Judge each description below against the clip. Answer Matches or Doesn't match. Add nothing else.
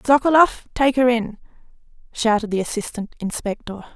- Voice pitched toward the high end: Matches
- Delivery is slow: Matches